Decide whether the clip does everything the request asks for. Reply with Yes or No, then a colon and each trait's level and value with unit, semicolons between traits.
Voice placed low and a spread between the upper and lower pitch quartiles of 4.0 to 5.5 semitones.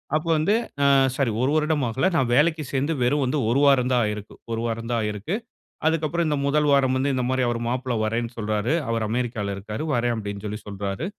Yes: low, 125 Hz; average, 4.4 semitones